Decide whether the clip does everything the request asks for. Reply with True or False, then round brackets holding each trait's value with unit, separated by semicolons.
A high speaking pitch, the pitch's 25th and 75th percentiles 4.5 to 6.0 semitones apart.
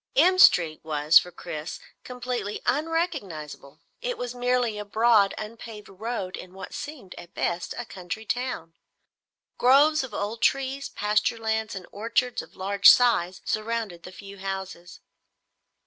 True (215 Hz; 5.0 semitones)